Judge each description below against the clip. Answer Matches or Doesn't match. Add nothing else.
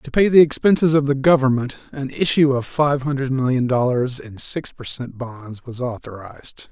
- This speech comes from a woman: Doesn't match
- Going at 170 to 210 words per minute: Matches